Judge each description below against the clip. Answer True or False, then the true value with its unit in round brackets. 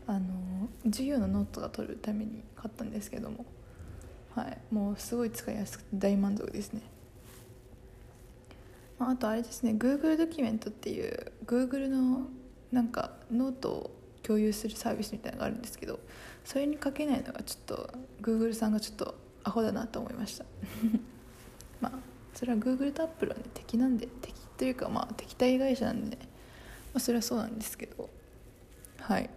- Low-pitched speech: False (235 Hz)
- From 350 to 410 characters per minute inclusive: True (385 characters per minute)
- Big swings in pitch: False (3.0 semitones)